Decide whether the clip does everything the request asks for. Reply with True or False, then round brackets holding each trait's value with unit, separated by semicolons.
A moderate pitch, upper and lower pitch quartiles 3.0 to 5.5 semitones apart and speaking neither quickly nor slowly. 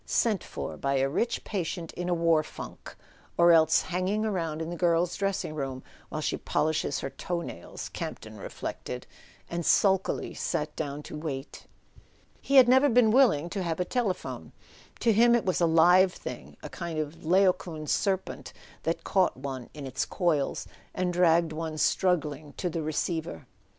True (170 Hz; 3.4 semitones; 170 wpm)